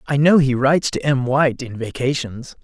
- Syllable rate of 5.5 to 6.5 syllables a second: No, 5.3 syllables/s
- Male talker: Yes, male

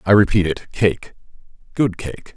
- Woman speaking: No, male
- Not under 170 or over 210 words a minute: No, slow, 125 wpm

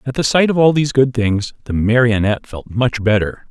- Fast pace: Yes, fast, 225 wpm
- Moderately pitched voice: No, low, 120 Hz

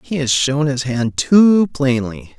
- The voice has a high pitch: No, medium, 140 Hz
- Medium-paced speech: Yes, average, 175 wpm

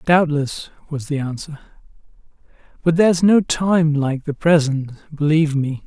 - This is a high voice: No, medium, 155 Hz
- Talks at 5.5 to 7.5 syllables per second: No, 4.6 syllables/s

